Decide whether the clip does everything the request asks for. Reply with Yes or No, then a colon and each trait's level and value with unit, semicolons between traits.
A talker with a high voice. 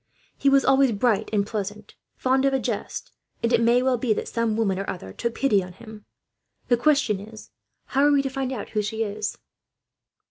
Yes: high, 230 Hz